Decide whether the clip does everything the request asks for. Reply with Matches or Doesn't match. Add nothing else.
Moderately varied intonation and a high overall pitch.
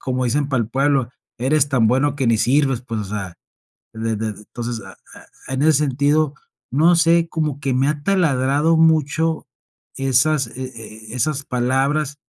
Doesn't match